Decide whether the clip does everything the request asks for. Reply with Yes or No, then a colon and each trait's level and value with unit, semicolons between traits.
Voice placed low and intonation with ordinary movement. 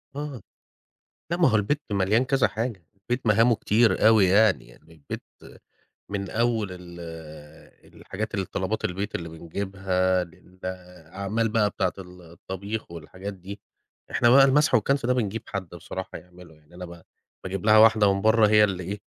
Yes: low, 100 Hz; average, 3.4 semitones